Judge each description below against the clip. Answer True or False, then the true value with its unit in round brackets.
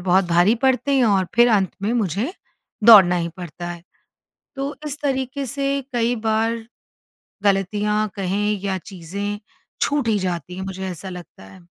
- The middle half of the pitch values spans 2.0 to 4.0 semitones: False (4.5 semitones)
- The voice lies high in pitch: True (205 Hz)